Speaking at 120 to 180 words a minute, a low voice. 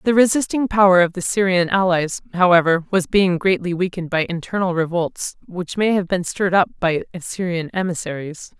No: average, 170 wpm; medium, 180 Hz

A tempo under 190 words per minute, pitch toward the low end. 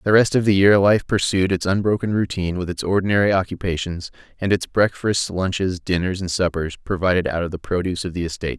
No: fast, 205 wpm; very low, 95 Hz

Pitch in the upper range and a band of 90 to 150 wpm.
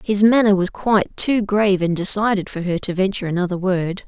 No: high, 195 Hz; fast, 205 wpm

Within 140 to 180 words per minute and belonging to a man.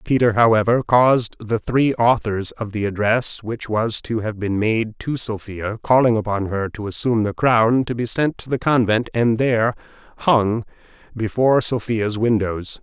Yes: average, 170 wpm; male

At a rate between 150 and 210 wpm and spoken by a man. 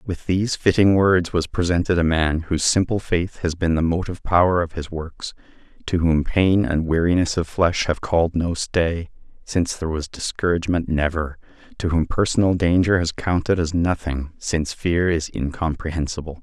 Yes: average, 170 wpm; male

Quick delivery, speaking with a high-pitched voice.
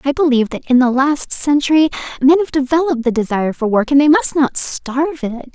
Yes: fast, 215 wpm; very high, 275 Hz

